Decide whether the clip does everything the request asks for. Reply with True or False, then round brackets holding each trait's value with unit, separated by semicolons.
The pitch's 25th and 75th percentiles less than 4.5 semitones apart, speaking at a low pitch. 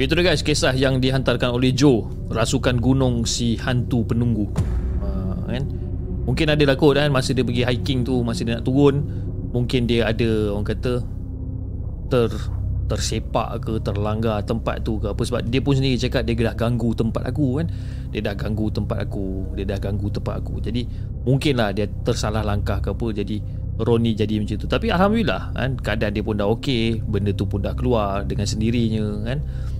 True (3.4 semitones; 115 Hz)